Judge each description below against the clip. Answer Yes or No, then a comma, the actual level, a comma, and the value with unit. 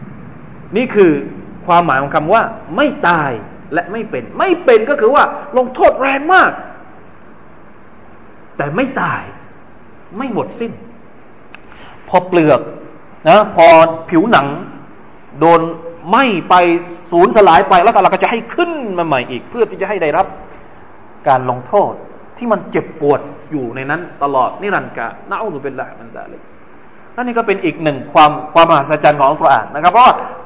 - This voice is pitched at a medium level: Yes, medium, 175 Hz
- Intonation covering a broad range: Yes, wide, 6.3 semitones